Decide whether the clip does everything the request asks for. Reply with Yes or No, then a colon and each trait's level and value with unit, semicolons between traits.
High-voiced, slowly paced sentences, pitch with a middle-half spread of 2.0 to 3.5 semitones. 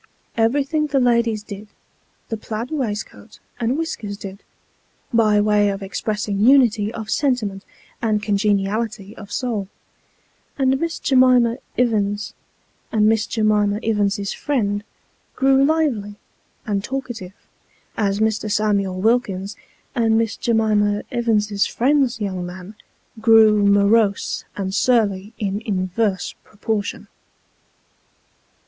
Yes: high, 215 Hz; slow, 110 wpm; narrow, 2.6 semitones